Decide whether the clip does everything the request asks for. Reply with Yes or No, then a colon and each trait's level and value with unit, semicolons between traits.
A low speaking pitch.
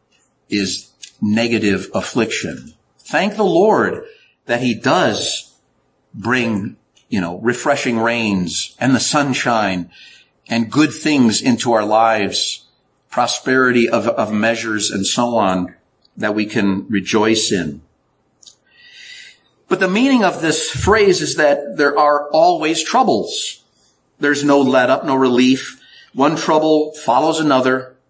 Yes: low, 130 Hz